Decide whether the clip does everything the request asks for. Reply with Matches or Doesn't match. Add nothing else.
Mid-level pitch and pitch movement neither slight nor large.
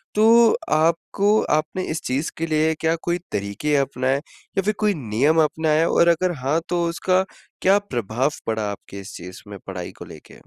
Doesn't match